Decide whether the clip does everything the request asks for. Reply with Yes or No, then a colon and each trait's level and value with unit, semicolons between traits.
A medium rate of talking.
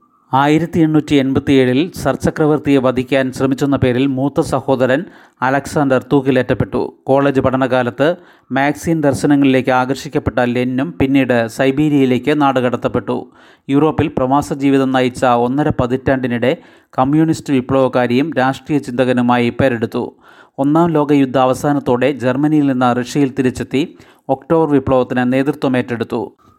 Yes: average, 95 wpm